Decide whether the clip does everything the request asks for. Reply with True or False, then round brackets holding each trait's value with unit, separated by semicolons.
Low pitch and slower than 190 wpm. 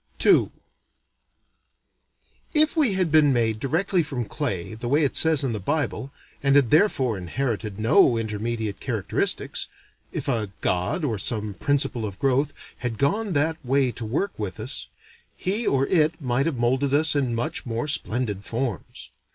True (130 Hz; 160 wpm)